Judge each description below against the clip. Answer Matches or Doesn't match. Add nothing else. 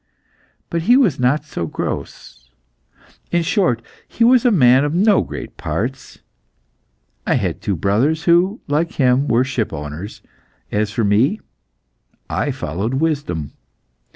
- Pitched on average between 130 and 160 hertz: Matches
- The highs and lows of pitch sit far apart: Matches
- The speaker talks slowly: Matches